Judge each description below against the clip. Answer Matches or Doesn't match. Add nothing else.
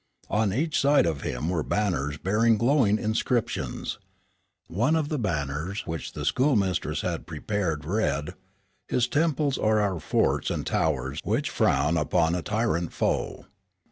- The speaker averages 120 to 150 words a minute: Matches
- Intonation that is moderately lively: Doesn't match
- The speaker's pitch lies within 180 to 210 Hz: Doesn't match